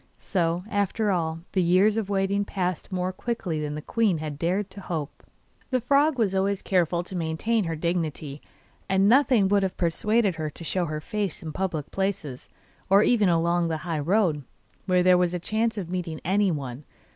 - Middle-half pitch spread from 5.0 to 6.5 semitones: No, average, 3.6 semitones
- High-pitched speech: No, medium, 180 Hz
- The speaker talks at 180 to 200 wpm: Yes, average, 185 wpm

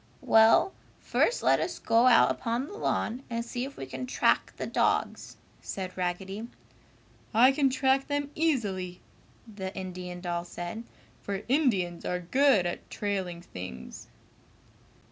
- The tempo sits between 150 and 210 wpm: No, average, 140 wpm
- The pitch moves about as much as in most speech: No, wide, 6.3 semitones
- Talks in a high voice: Yes, high, 215 Hz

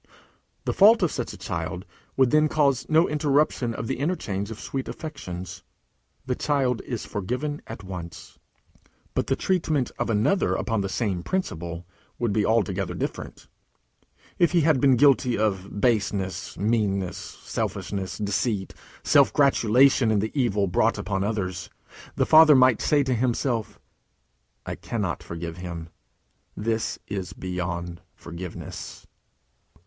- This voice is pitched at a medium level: No, low, 110 Hz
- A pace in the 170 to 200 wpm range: No, slow, 135 wpm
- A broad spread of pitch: Yes, wide, 6.4 semitones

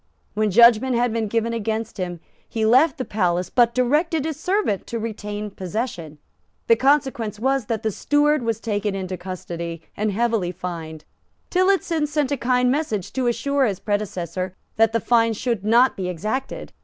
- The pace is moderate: Yes, average, 170 wpm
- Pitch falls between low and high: No, high, 225 Hz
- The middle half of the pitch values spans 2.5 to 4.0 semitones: No, average, 4.7 semitones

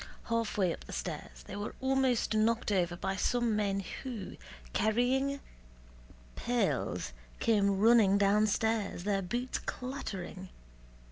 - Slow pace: Yes, slow, 115 wpm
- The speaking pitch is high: Yes, high, 215 Hz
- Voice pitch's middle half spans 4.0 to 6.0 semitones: No, average, 3.5 semitones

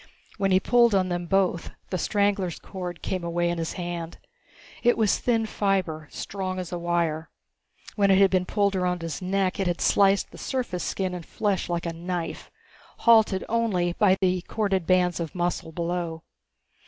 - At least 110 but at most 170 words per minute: No, average, 180 wpm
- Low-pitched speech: No, medium, 185 Hz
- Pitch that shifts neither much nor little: No, narrow, 2.3 semitones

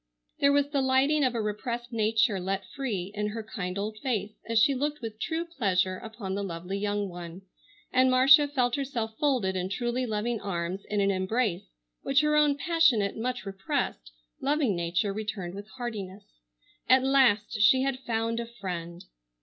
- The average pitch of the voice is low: No, high, 220 Hz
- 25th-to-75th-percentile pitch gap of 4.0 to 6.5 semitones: Yes, average, 4.9 semitones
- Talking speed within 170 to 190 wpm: Yes, average, 175 wpm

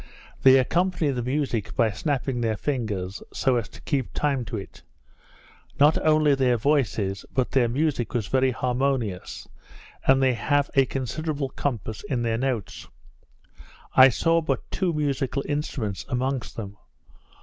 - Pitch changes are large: No, average, 3.7 semitones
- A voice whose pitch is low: Yes, low, 130 Hz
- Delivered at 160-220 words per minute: No, average, 145 wpm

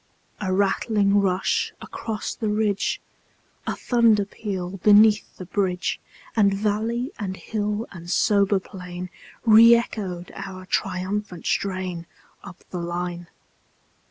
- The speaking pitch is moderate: No, high, 200 Hz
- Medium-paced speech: No, slow, 115 wpm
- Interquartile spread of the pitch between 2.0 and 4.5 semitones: Yes, narrow, 2.5 semitones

